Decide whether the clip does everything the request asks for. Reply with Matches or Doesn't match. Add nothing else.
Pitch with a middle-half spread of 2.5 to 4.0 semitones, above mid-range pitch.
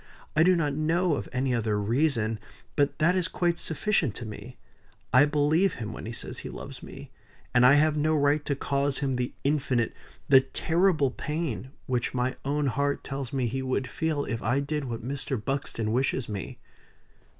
Doesn't match